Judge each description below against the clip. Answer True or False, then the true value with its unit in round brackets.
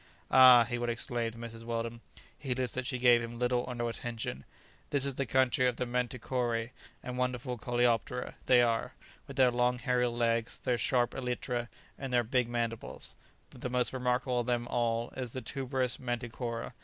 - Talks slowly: False (180 wpm)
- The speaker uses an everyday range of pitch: False (1.2 semitones)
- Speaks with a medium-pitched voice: False (120 Hz)